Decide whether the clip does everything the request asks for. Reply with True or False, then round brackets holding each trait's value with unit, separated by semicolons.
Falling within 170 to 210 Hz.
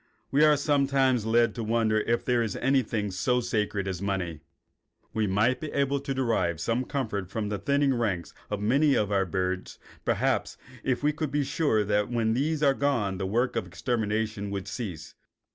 False (115 Hz)